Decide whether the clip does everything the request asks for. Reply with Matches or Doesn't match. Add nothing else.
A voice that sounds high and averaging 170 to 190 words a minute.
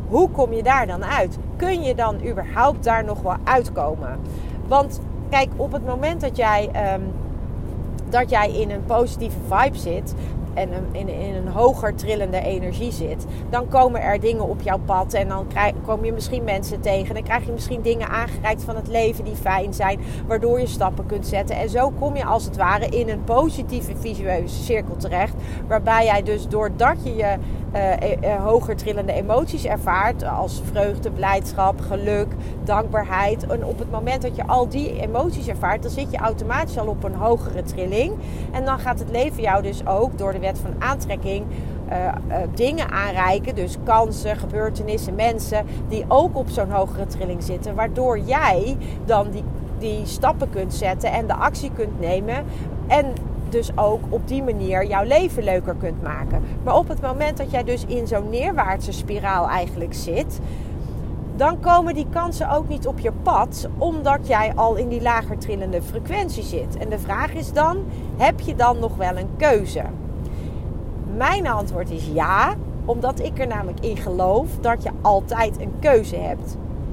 Matches